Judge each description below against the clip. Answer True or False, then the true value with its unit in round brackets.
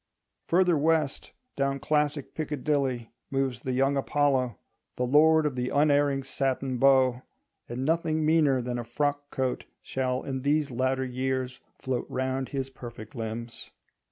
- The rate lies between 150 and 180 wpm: False (140 wpm)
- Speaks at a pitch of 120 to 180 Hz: True (135 Hz)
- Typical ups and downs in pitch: False (2.2 semitones)